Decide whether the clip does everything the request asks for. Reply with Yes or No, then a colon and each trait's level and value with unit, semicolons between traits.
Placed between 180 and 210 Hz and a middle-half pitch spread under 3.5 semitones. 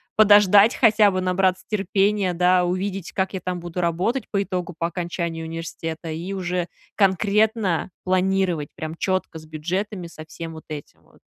Yes: medium, 185 Hz; average, 2.8 semitones